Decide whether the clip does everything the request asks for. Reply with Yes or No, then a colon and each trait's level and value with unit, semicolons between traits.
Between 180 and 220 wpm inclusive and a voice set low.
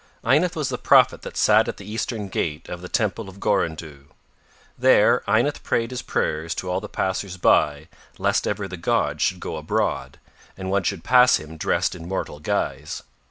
Yes: average, 185 wpm; very low, 95 Hz